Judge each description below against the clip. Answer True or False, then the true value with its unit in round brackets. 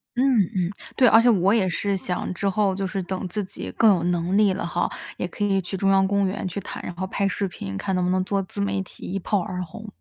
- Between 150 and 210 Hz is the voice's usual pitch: True (190 Hz)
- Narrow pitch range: True (1.7 semitones)